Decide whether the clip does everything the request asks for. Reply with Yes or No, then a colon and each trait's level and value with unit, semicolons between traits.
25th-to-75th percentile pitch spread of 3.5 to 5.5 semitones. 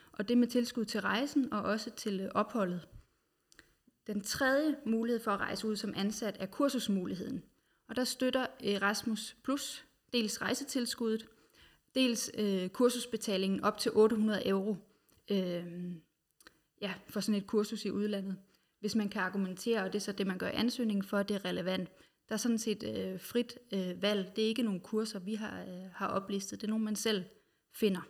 No: average, 2.9 semitones